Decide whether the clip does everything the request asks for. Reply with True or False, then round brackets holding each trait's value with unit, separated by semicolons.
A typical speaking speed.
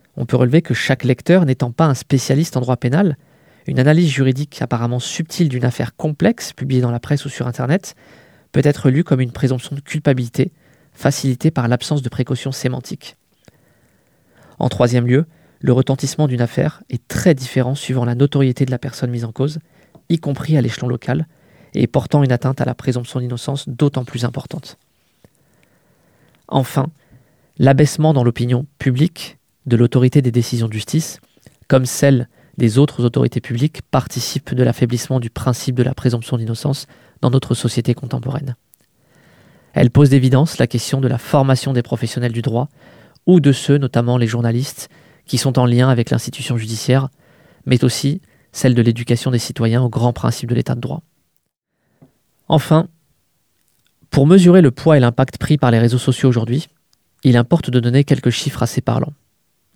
True (170 wpm)